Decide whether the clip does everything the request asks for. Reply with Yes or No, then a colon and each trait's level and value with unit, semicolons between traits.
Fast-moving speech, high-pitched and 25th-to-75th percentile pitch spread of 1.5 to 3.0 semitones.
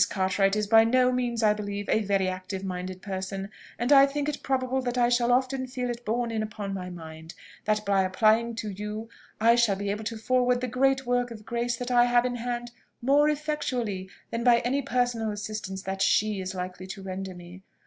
No: fast, 210 wpm; high, 225 Hz; average, 4.0 semitones